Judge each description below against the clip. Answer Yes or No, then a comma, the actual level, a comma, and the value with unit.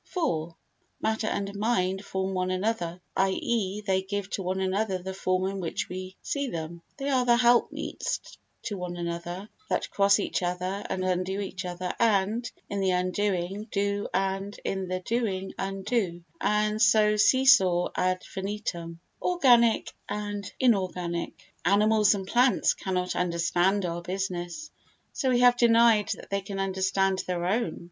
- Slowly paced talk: No, average, 155 wpm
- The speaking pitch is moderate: No, high, 195 Hz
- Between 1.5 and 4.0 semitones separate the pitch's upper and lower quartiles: Yes, narrow, 2.6 semitones